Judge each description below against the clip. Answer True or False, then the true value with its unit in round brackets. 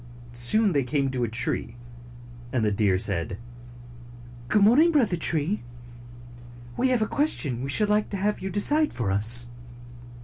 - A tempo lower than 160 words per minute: False (165 wpm)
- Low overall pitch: False (145 Hz)